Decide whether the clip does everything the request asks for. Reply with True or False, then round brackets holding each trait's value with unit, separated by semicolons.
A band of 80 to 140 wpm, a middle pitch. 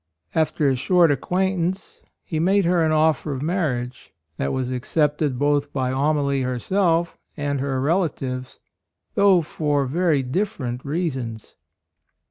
True (135 wpm; 145 Hz)